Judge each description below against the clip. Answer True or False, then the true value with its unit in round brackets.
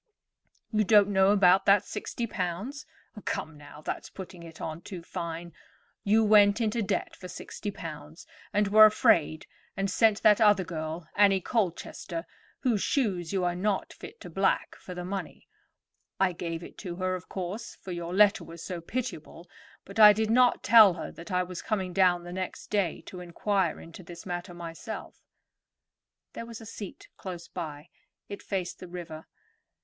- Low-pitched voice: False (185 Hz)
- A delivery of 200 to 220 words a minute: False (175 wpm)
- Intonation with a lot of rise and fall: False (3.2 semitones)